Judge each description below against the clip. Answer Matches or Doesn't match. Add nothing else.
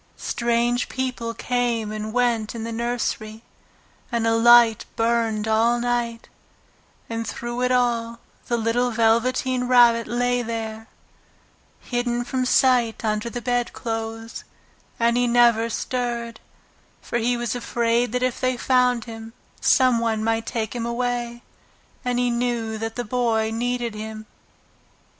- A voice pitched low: Doesn't match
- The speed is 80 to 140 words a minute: Matches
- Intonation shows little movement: Matches